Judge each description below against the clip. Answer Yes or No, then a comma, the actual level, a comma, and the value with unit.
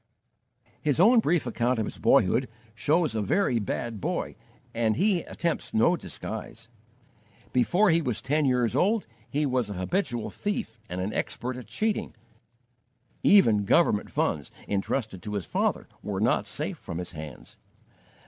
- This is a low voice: Yes, low, 125 Hz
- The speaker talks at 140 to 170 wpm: Yes, average, 150 wpm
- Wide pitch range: Yes, wide, 7.9 semitones